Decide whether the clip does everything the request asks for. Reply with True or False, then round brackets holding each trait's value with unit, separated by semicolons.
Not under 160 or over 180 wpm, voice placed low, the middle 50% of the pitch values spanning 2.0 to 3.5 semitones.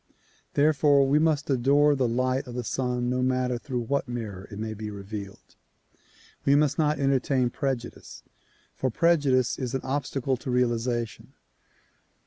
False (145 wpm; 130 Hz; 2.8 semitones)